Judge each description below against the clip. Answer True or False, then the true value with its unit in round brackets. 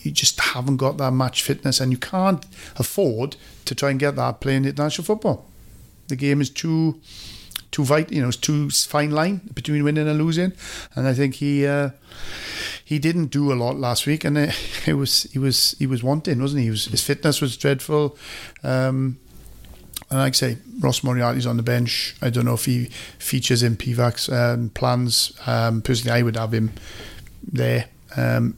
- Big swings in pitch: False (3.2 semitones)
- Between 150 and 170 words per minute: False (195 wpm)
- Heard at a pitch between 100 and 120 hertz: False (135 Hz)